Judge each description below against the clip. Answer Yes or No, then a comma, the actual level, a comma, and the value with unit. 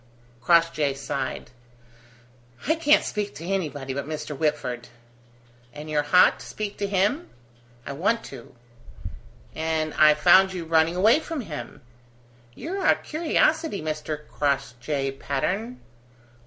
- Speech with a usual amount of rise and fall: No, wide, 5.8 semitones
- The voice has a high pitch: No, medium, 160 Hz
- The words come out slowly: Yes, slow, 125 wpm